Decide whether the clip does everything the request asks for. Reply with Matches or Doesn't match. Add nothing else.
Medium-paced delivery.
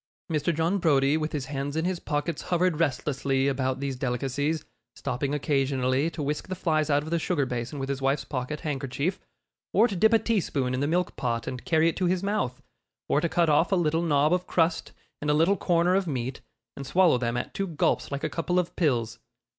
Doesn't match